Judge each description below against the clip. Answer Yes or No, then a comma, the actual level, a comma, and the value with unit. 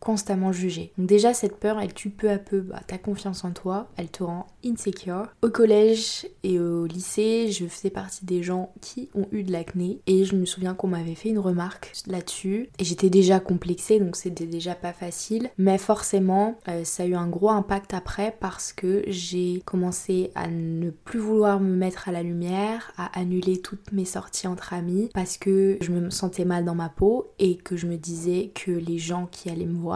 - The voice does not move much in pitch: Yes, narrow, 2.2 semitones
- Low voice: No, medium, 185 Hz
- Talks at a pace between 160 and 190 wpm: No, average, 210 wpm